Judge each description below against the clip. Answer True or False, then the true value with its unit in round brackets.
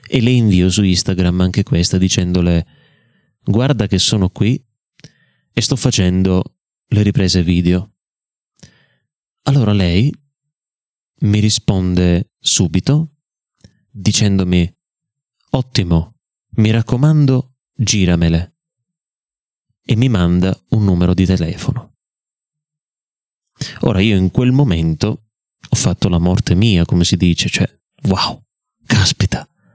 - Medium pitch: False (105 Hz)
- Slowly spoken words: True (105 wpm)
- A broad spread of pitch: True (5.7 semitones)